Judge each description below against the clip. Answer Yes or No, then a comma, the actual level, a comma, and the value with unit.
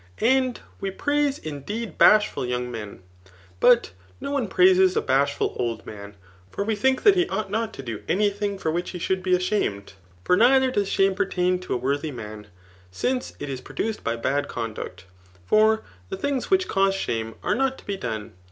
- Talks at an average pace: Yes, average, 195 wpm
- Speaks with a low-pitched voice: No, high, 190 Hz